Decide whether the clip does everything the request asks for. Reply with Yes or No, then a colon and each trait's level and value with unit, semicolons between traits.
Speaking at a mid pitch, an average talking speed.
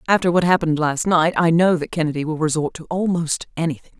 No: medium, 165 Hz; fast, 210 wpm